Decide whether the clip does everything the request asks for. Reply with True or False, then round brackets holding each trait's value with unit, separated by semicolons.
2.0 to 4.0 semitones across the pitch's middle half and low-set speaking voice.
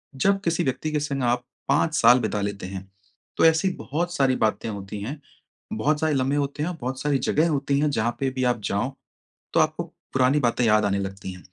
False (5.4 semitones; 130 Hz)